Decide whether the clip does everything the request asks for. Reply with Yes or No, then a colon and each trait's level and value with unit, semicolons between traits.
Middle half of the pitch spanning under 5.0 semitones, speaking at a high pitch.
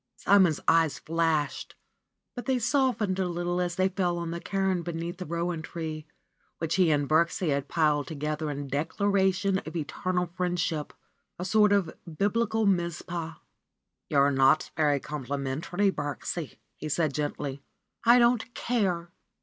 No: average, 3.8 semitones; medium, 170 Hz